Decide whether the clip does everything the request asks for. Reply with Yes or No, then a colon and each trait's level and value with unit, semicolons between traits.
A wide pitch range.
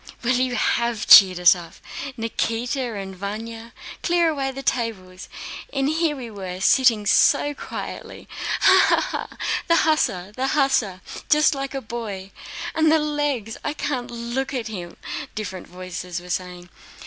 Yes: wide, 6.1 semitones